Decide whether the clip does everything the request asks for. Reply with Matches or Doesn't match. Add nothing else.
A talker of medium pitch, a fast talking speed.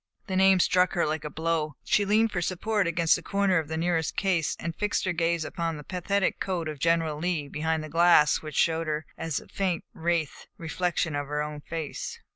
Matches